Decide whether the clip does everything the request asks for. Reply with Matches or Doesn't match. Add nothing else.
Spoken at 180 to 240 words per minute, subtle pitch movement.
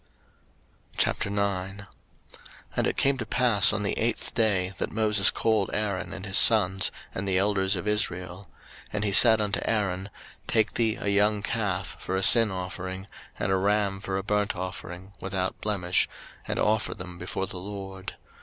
Doesn't match